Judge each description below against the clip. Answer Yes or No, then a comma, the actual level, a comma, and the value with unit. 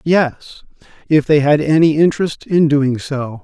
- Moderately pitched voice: Yes, medium, 150 Hz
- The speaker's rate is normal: Yes, average, 155 wpm